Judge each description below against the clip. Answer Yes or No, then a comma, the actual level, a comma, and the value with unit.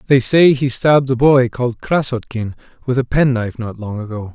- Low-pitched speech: Yes, low, 125 Hz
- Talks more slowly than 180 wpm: No, fast, 205 wpm